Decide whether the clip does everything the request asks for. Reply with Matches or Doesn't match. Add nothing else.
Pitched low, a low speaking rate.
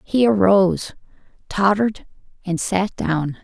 Doesn't match